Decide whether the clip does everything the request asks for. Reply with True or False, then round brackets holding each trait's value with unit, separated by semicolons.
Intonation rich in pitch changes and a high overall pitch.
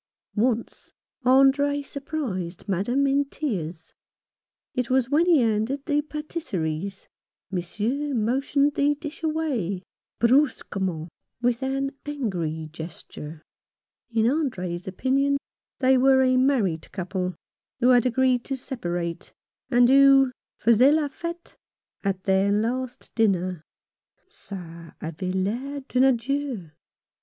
True (6.6 semitones; 245 Hz)